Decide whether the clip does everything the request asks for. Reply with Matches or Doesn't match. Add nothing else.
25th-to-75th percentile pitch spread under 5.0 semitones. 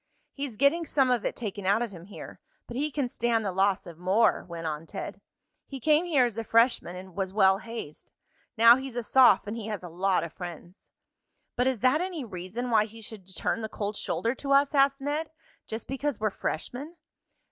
Doesn't match